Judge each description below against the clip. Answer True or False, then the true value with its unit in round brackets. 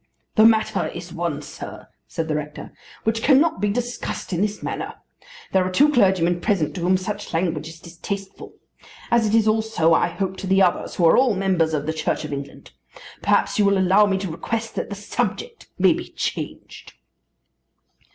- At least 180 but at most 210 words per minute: True (190 wpm)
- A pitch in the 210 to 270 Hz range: False (190 Hz)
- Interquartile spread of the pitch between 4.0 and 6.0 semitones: True (4.3 semitones)